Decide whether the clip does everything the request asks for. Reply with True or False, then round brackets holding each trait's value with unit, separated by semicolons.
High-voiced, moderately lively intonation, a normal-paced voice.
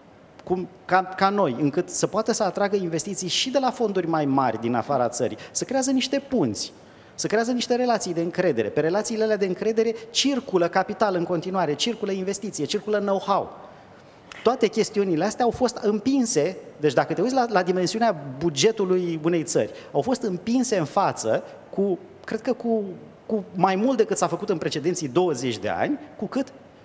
False (200 Hz; 4.4 semitones; 180 wpm)